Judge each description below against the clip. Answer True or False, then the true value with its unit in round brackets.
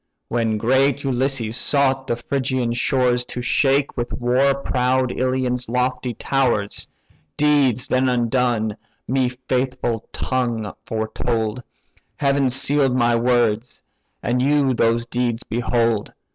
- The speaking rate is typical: False (115 wpm)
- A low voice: True (125 Hz)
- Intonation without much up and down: True (2.0 semitones)